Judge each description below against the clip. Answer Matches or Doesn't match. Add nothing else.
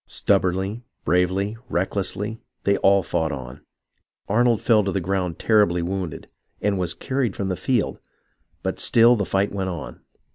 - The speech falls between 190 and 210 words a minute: Doesn't match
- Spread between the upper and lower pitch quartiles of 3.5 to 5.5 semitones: Doesn't match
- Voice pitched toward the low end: Matches